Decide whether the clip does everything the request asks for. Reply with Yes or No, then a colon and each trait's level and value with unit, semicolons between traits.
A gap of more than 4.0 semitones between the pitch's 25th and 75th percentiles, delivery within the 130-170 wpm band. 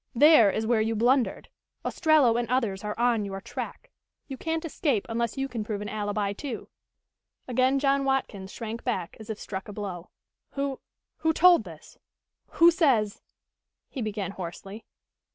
Yes: average, 4.7 semitones; average, 165 wpm